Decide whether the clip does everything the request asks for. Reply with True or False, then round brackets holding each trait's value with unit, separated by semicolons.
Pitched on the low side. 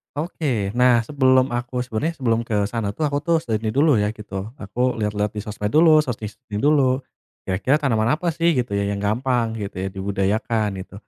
True (115 Hz)